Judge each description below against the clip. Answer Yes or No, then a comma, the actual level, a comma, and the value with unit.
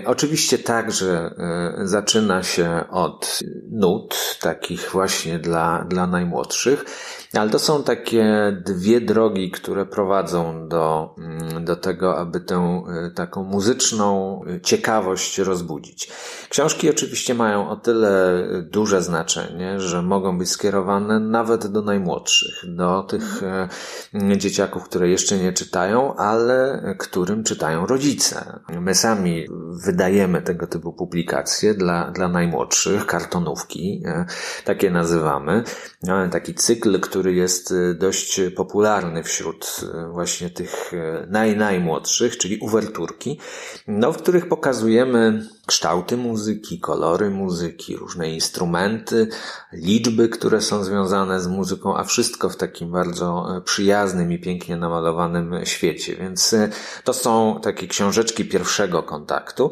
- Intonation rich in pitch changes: No, average, 3.5 semitones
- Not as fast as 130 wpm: Yes, average, 115 wpm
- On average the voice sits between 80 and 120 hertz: Yes, very low, 95 Hz